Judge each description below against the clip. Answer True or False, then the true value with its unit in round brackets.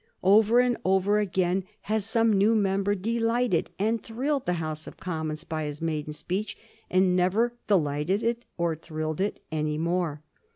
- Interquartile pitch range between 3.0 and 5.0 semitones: False (5.4 semitones)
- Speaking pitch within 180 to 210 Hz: True (190 Hz)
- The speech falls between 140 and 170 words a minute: True (160 wpm)